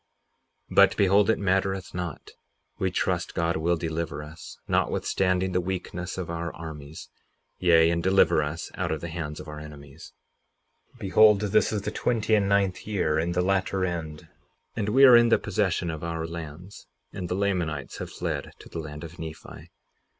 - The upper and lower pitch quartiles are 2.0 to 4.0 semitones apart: Yes, average, 3.3 semitones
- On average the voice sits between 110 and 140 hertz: No, very low, 90 Hz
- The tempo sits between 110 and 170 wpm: No, average, 180 wpm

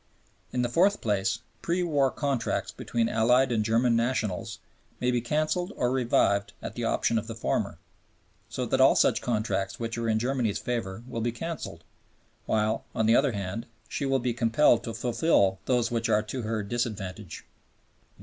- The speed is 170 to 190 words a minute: Yes, average, 175 wpm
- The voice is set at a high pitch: No, low, 115 Hz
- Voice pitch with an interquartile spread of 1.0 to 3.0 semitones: Yes, narrow, 2.5 semitones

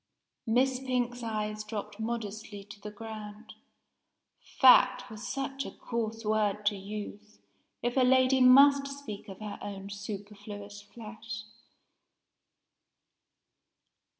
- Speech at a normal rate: No, slow, 110 wpm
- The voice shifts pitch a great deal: No, average, 3.2 semitones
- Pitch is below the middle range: No, high, 215 Hz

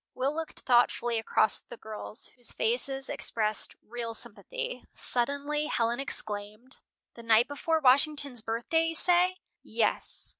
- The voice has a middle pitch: No, very high, 250 Hz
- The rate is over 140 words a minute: No, slow, 135 wpm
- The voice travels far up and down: No, average, 4.6 semitones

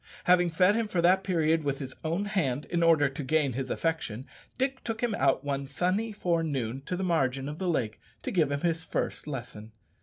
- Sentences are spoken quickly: Yes, fast, 210 wpm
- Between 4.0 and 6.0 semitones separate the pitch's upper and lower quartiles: Yes, average, 5.0 semitones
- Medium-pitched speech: Yes, medium, 160 Hz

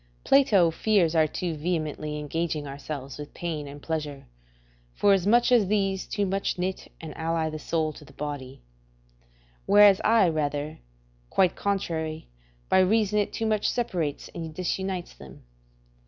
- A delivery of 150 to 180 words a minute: No, average, 140 wpm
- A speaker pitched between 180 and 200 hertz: No, medium, 165 Hz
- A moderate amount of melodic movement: Yes, average, 4.5 semitones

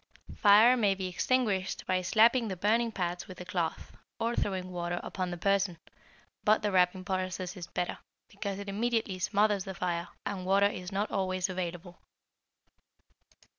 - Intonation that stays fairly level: Yes, narrow, 2.3 semitones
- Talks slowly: No, average, 160 wpm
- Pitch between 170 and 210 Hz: Yes, high, 190 Hz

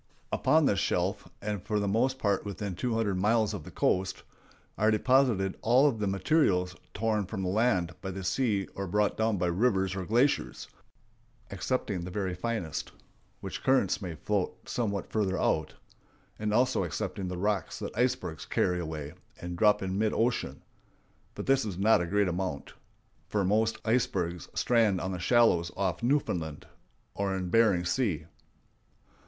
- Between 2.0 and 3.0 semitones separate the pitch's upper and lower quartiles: No, average, 3.7 semitones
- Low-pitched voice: Yes, low, 100 Hz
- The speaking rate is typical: Yes, average, 165 wpm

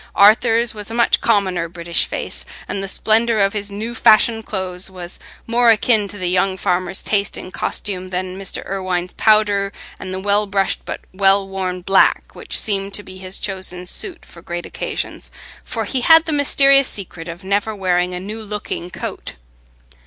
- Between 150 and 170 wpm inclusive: No, average, 180 wpm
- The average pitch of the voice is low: No, high, 195 Hz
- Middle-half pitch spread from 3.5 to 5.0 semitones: No, average, 2.8 semitones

